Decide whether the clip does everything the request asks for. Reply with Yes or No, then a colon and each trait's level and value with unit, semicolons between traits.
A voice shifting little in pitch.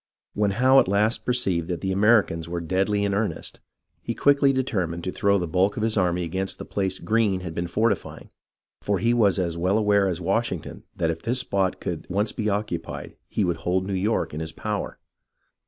No: average, 3.3 semitones